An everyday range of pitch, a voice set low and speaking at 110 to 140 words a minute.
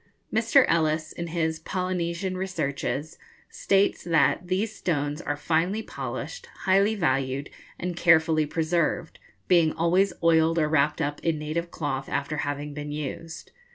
No: average, 3.2 semitones; medium, 165 Hz; slow, 135 wpm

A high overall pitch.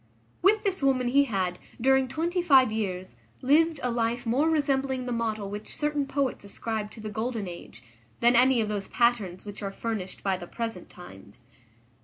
Yes: high, 235 Hz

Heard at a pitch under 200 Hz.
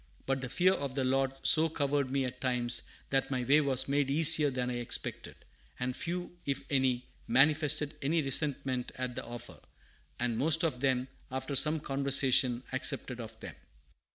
Yes: low, 135 Hz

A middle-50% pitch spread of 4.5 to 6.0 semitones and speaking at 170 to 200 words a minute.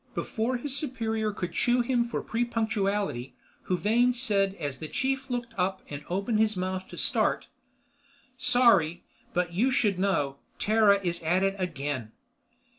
No: average, 4.9 semitones; average, 145 wpm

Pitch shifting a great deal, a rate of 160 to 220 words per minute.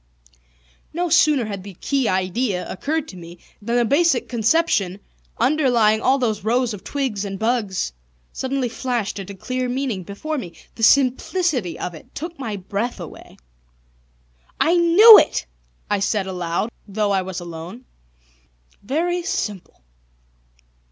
No: wide, 6.1 semitones; average, 140 wpm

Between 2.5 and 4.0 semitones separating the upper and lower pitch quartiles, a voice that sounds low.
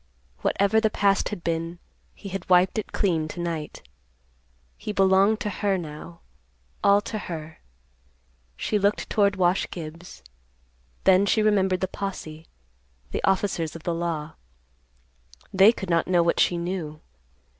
No: average, 3.1 semitones; medium, 185 Hz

